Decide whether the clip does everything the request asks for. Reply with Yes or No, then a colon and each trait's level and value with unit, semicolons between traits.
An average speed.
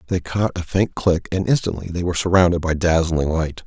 No: fast, 215 wpm